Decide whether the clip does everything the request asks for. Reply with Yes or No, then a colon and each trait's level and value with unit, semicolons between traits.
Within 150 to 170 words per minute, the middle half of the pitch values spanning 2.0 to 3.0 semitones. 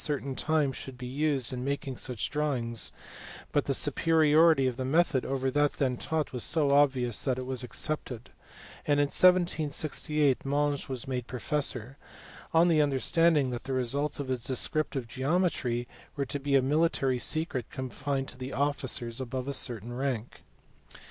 Yes: average, 160 wpm; average, 2.7 semitones